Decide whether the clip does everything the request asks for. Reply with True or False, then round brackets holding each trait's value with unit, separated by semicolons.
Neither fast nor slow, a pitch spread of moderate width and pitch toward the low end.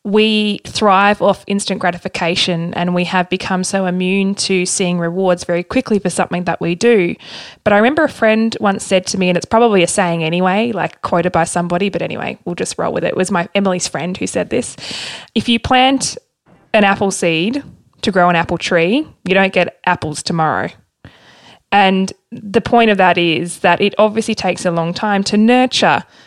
False (195 wpm; 3.2 semitones; 190 Hz)